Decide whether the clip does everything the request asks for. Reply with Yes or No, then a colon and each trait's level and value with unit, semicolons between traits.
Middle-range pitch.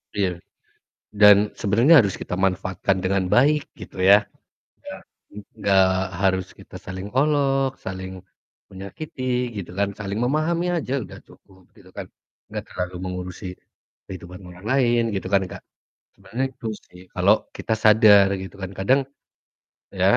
No: low, 100 Hz